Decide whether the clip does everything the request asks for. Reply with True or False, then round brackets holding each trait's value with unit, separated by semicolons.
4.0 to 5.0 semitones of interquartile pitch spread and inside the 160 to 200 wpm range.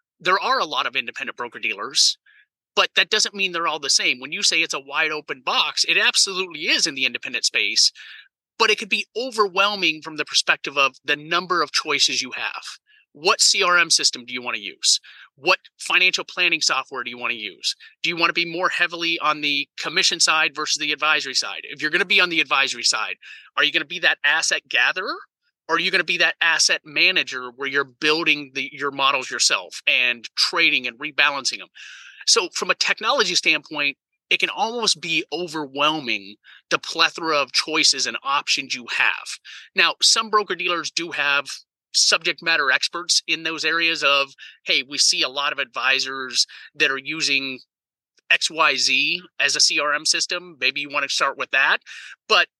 True (4.5 semitones; 195 wpm)